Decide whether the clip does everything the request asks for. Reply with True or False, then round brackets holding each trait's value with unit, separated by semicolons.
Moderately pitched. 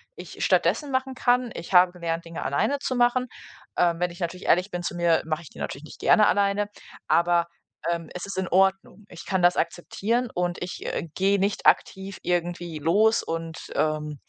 True (180 Hz)